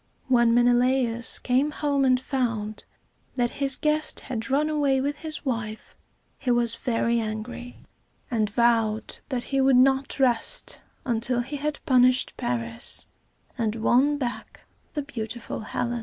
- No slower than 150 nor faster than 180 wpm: No, average, 140 wpm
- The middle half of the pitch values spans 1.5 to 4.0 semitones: Yes, average, 2.8 semitones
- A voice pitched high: Yes, high, 245 Hz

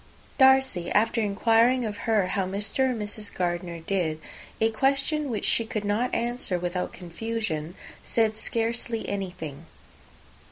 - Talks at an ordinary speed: No, slow, 130 wpm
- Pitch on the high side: Yes, high, 215 Hz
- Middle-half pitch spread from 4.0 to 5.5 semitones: Yes, average, 4.3 semitones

